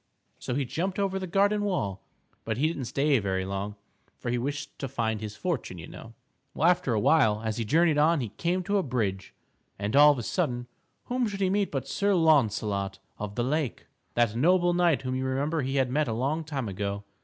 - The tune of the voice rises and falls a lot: Yes, wide, 7.3 semitones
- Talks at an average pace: No, fast, 220 wpm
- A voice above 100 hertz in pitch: Yes, low, 135 Hz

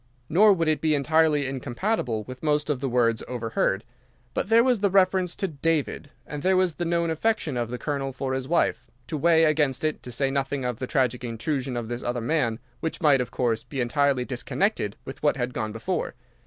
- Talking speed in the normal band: No, fast, 210 wpm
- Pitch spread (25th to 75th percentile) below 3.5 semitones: No, average, 4.6 semitones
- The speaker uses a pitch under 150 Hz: Yes, medium, 140 Hz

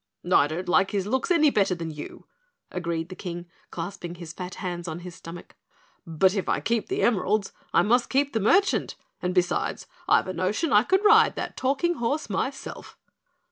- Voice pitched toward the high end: Yes, high, 195 Hz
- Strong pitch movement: Yes, wide, 7.0 semitones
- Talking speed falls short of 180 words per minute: No, average, 185 wpm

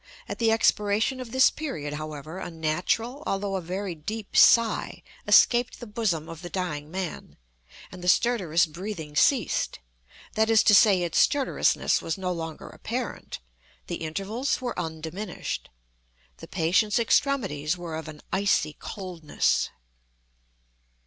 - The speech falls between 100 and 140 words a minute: Yes, slow, 135 wpm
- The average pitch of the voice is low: No, medium, 185 Hz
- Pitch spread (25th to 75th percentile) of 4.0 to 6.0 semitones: Yes, wide, 5.5 semitones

